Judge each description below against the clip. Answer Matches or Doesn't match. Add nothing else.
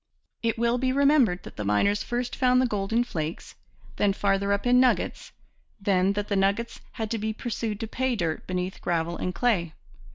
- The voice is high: Matches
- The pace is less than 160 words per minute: Doesn't match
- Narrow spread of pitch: Doesn't match